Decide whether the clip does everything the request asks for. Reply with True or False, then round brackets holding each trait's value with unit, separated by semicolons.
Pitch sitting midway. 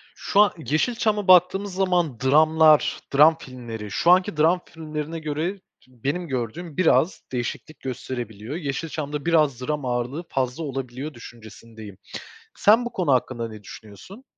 True (150 Hz)